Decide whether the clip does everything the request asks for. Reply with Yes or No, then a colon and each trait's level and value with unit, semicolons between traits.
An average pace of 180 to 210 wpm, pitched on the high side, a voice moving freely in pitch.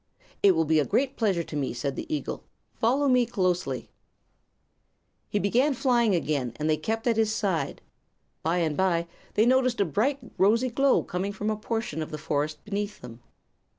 Yes: average, 185 wpm; high, 200 Hz; wide, 7.0 semitones